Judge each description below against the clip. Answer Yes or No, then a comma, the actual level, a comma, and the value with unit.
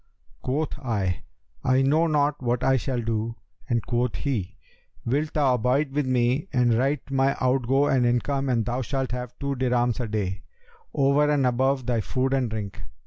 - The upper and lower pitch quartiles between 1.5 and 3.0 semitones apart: Yes, narrow, 2.4 semitones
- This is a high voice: No, low, 130 Hz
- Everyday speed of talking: Yes, average, 175 wpm